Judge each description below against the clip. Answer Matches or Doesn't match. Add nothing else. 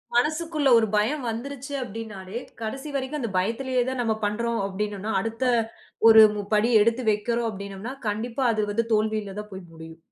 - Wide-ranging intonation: Doesn't match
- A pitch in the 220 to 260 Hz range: Matches